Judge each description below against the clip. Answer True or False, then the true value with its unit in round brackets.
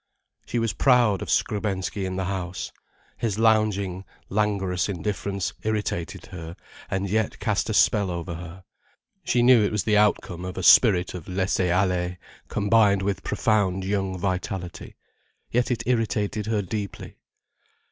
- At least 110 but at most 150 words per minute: True (145 wpm)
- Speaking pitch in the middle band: False (100 Hz)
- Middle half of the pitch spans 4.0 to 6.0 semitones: False (2.7 semitones)